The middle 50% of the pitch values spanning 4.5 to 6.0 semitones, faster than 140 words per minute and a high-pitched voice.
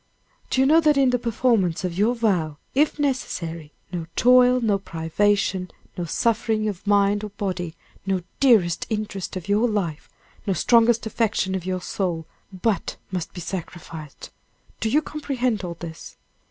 Yes: average, 4.9 semitones; average, 155 wpm; high, 205 Hz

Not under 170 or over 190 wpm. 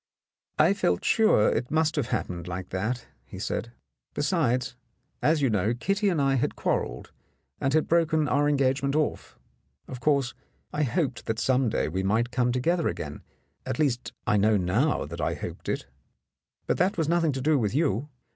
Yes: average, 185 wpm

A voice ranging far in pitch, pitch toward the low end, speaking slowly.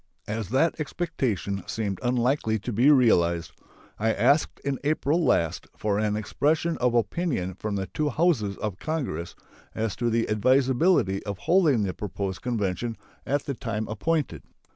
No: wide, 5.8 semitones; low, 115 Hz; average, 150 wpm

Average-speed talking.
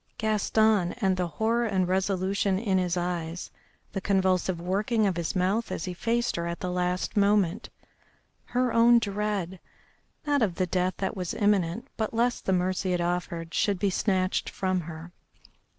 Yes: average, 165 wpm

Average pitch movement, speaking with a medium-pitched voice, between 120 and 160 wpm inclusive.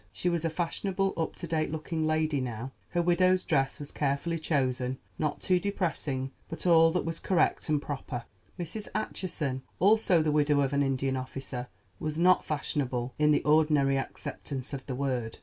No: average, 3.9 semitones; medium, 150 Hz; average, 170 wpm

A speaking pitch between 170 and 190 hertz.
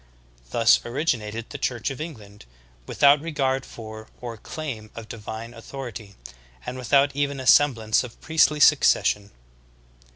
No: low, 125 Hz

